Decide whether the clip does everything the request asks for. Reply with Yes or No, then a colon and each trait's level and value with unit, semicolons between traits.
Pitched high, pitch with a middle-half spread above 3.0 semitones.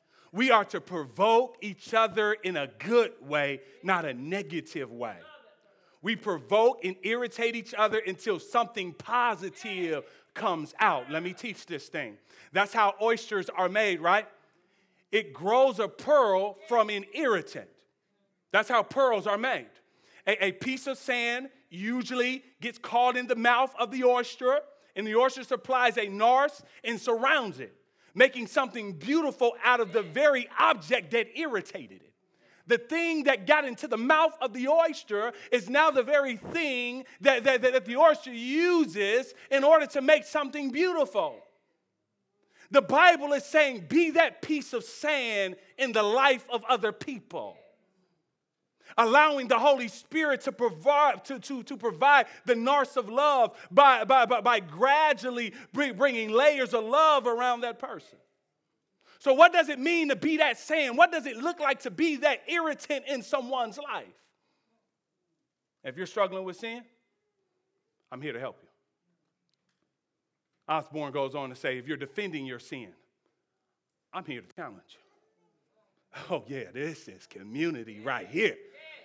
Yes: high, 245 Hz; average, 5.3 semitones